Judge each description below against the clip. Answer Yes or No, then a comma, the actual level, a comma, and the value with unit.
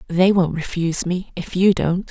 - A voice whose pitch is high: No, medium, 180 Hz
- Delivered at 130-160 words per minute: No, average, 200 wpm